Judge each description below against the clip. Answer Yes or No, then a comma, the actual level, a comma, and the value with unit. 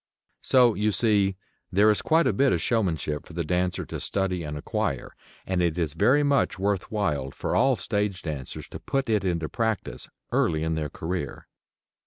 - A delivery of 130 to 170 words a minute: No, average, 185 wpm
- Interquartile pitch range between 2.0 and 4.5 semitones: No, average, 5.1 semitones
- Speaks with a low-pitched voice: Yes, very low, 95 Hz